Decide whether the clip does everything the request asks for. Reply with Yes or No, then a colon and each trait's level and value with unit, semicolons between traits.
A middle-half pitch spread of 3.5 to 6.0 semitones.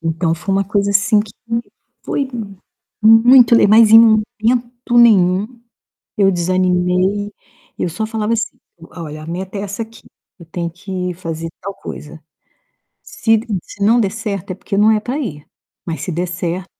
Yes: average, 3.9 semitones